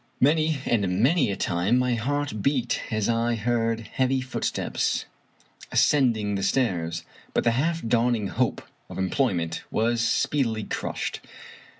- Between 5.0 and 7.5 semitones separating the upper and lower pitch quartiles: No, average, 3.7 semitones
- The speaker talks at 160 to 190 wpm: No, average, 140 wpm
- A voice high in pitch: No, low, 115 Hz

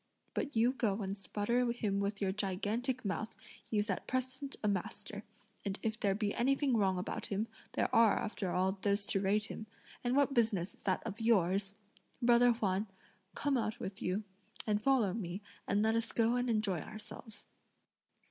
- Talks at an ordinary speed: Yes, average, 175 wpm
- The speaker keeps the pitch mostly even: No, average, 3.1 semitones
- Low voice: No, high, 215 Hz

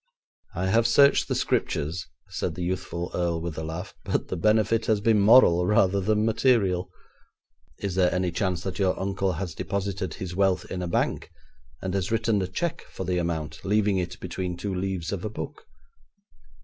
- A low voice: Yes, very low, 95 Hz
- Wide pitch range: No, average, 2.7 semitones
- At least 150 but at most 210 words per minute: Yes, average, 185 wpm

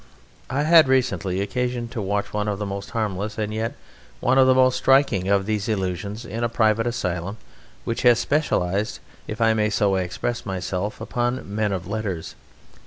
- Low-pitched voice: Yes, low, 110 Hz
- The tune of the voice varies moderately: Yes, average, 3.6 semitones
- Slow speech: No, average, 175 wpm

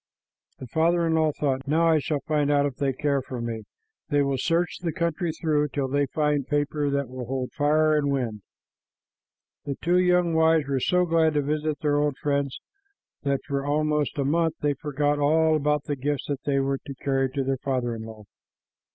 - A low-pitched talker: No, medium, 145 Hz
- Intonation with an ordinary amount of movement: No, narrow, 2.3 semitones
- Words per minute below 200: No, fast, 205 wpm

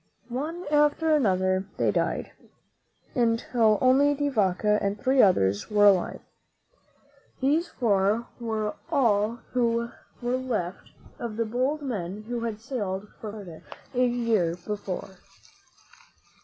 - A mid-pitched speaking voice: No, high, 230 Hz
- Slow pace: Yes, slow, 120 wpm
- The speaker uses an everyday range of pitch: Yes, average, 4.1 semitones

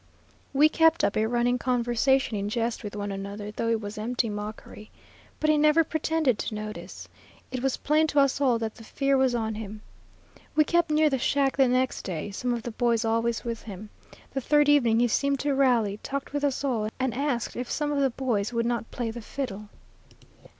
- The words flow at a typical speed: No, fast, 210 wpm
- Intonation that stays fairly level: No, average, 4.1 semitones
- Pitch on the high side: Yes, high, 240 Hz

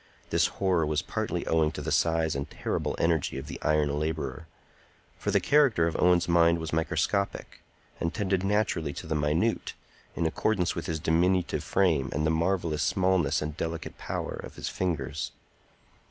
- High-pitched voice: No, very low, 80 Hz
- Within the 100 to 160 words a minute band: No, average, 170 wpm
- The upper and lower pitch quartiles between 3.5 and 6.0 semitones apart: No, average, 2.8 semitones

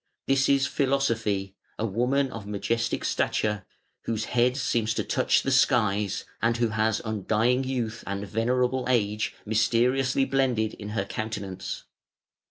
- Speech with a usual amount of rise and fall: Yes, average, 3.3 semitones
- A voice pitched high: No, low, 115 Hz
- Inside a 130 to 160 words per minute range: Yes, slow, 135 wpm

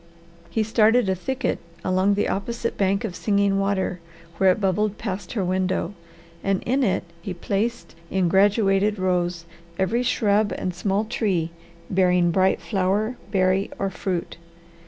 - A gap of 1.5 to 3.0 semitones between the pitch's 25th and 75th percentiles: Yes, narrow, 2.4 semitones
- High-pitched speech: Yes, high, 195 Hz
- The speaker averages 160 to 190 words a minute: No, average, 145 wpm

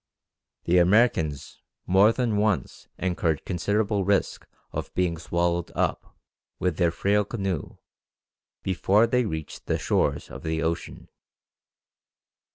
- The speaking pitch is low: Yes, very low, 90 Hz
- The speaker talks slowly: Yes, slow, 115 wpm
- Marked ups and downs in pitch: No, average, 3.7 semitones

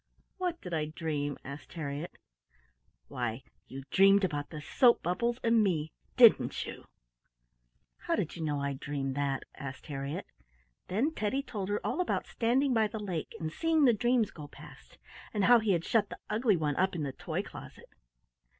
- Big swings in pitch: Yes, wide, 7.6 semitones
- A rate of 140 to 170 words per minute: No, average, 180 wpm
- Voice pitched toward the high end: No, medium, 180 Hz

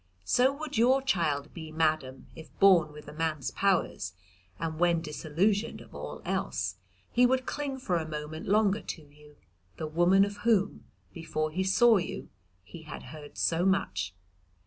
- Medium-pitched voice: Yes, medium, 165 Hz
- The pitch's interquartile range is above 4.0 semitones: Yes, average, 4.8 semitones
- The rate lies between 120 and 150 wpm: No, average, 165 wpm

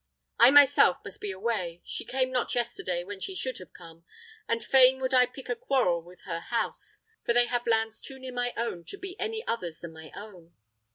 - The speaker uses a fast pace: Yes, fast, 215 wpm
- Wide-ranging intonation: Yes, wide, 6.3 semitones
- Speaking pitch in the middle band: No, high, 235 Hz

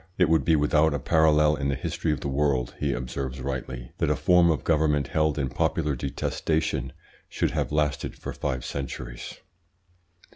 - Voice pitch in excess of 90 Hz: No, very low, 75 Hz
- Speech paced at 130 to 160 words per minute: No, average, 175 wpm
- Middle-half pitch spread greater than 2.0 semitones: Yes, average, 2.9 semitones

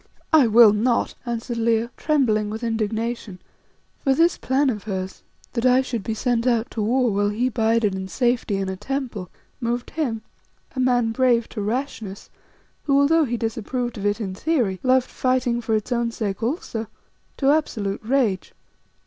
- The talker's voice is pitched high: Yes, high, 235 Hz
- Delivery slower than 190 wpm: Yes, average, 170 wpm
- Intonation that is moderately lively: Yes, average, 3.1 semitones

